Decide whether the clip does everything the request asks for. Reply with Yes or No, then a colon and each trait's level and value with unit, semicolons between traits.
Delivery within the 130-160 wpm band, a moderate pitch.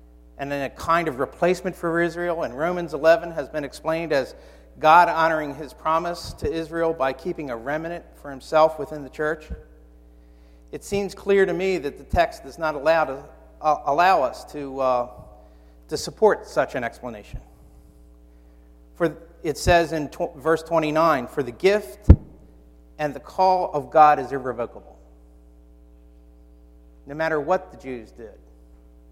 Yes: average, 155 wpm; medium, 145 Hz